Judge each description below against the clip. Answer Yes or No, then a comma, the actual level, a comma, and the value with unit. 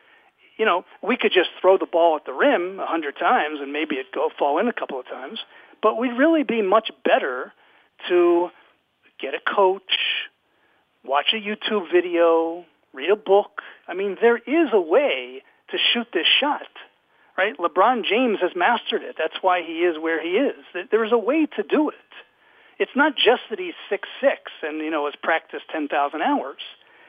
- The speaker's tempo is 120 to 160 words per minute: No, average, 190 wpm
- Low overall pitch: No, high, 215 Hz